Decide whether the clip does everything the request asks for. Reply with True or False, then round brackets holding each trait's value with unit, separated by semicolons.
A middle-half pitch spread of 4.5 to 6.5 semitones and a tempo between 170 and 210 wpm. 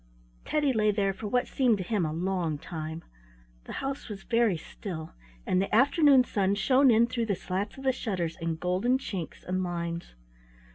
True (5.4 semitones; 185 wpm)